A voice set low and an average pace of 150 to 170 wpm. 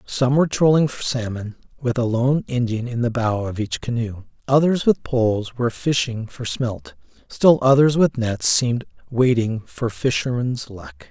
Yes: low, 120 Hz; average, 165 wpm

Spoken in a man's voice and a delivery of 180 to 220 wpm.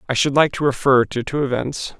No: male; fast, 240 wpm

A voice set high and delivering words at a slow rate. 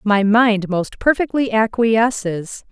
Yes: high, 220 Hz; slow, 110 wpm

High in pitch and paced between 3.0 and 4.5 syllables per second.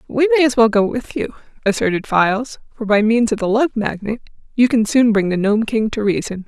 No: high, 225 Hz; 5.5 syllables/s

